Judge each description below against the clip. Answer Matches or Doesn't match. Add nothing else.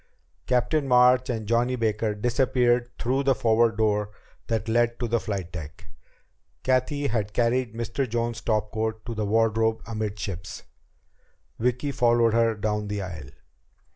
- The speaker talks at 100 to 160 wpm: Matches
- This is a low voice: Matches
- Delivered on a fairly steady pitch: Matches